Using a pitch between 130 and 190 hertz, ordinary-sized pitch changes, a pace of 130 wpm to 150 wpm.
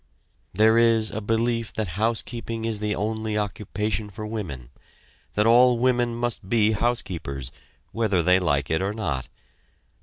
No: low, 110 Hz; average, 3.2 semitones; average, 145 wpm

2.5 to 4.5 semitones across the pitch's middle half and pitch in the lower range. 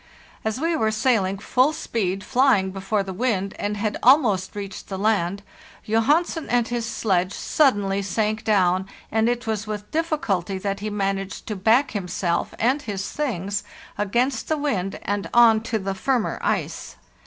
No: average, 3.6 semitones; high, 210 Hz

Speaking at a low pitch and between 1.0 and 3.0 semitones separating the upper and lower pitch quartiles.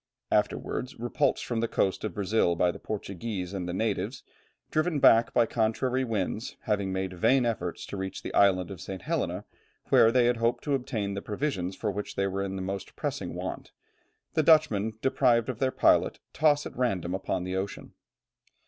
No: low, 110 Hz; average, 4.4 semitones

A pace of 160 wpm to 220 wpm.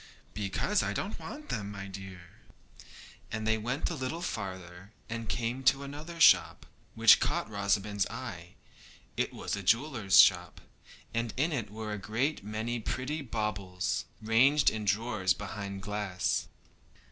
No: average, 140 wpm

